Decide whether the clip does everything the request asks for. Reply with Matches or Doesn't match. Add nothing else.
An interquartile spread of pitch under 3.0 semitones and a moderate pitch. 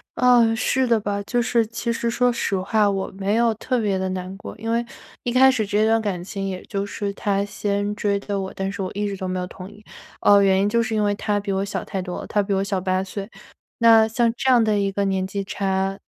Doesn't match